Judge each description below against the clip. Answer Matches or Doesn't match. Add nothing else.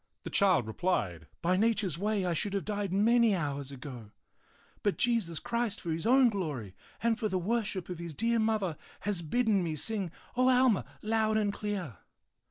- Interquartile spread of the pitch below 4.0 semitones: Doesn't match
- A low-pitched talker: Doesn't match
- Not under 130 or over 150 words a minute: Doesn't match